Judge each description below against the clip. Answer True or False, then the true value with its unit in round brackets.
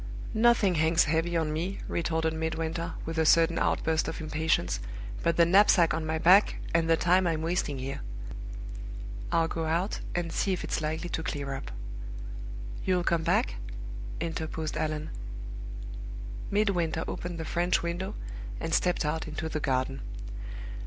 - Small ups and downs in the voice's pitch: True (1.5 semitones)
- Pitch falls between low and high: True (165 Hz)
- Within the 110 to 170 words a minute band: True (150 wpm)